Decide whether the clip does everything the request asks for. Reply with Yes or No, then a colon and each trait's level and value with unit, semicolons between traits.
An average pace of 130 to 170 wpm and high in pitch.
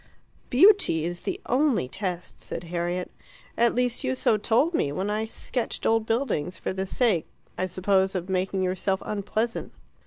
Yes: average, 160 wpm; high, 195 Hz